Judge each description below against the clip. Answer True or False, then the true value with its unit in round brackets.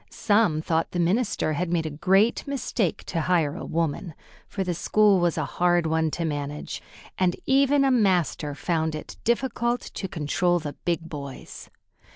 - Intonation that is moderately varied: True (4.4 semitones)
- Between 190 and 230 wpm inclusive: False (170 wpm)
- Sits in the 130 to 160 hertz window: False (175 Hz)